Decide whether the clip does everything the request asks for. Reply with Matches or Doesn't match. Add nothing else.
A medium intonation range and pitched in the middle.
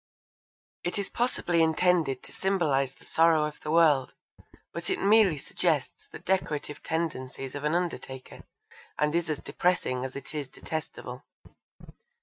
Matches